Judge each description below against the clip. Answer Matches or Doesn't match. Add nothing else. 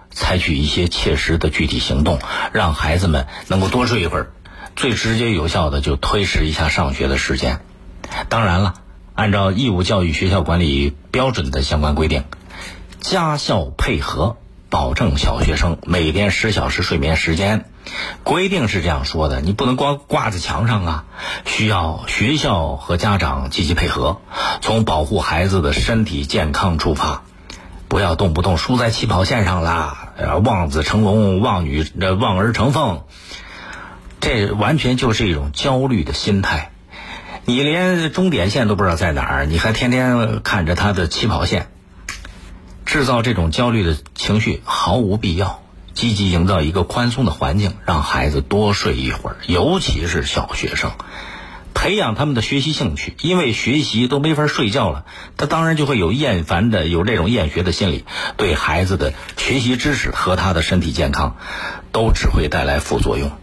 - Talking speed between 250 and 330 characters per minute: Matches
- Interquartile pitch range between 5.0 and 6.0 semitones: Matches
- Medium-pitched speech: Doesn't match